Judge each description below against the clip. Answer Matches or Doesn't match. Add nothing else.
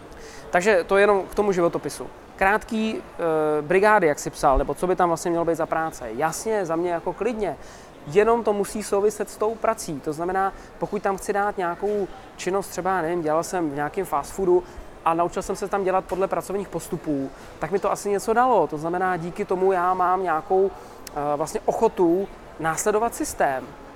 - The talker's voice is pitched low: Doesn't match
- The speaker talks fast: Matches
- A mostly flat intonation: Doesn't match